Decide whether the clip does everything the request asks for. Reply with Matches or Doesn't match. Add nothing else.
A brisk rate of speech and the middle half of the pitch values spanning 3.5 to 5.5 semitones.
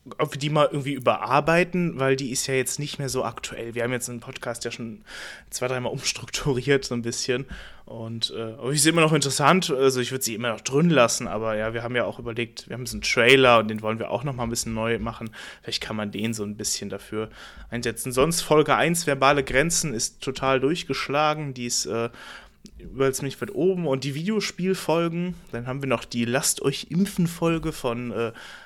Matches